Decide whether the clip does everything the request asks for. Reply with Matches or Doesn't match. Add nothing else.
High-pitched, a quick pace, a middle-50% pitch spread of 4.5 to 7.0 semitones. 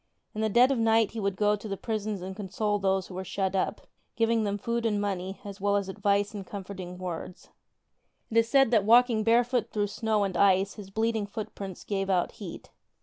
Doesn't match